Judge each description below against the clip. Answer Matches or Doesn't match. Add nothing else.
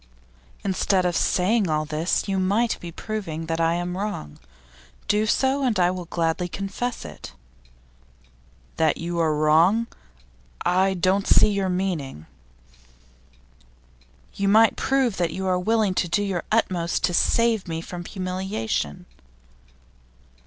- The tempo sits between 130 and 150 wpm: Matches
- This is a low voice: Doesn't match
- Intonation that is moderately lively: Matches